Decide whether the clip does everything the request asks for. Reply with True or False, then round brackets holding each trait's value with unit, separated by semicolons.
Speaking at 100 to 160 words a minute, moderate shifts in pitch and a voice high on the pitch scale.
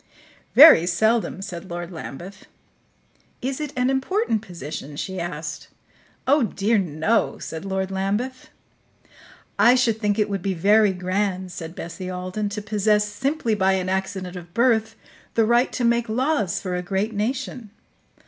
True (150 wpm; 4.1 semitones; 205 Hz)